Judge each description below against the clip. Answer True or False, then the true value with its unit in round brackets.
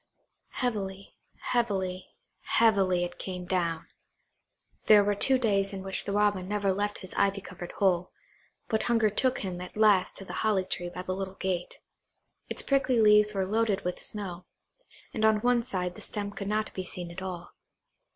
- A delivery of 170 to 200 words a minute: True (175 wpm)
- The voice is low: False (195 Hz)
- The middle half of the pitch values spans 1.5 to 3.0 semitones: True (2.5 semitones)